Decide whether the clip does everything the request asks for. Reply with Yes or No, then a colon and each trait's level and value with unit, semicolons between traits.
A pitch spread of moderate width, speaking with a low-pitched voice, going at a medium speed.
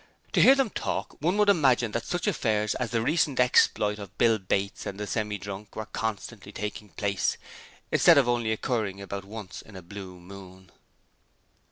Yes: average, 3.5 semitones; low, 105 Hz; average, 180 wpm